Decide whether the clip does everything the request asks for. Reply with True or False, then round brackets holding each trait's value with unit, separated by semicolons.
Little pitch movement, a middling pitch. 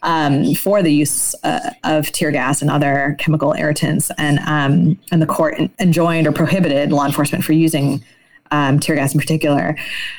True (1.9 semitones; 150 Hz)